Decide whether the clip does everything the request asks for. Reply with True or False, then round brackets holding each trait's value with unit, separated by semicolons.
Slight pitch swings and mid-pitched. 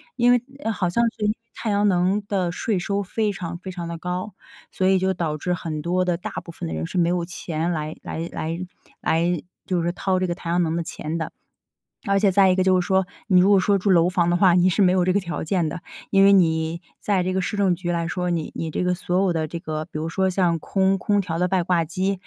True (2.1 semitones; 180 Hz)